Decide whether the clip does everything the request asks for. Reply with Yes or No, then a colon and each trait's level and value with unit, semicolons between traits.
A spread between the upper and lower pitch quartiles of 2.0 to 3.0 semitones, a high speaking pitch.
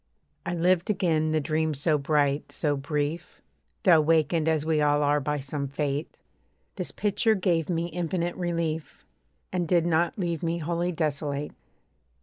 No: average, 2.7 semitones; medium, 160 Hz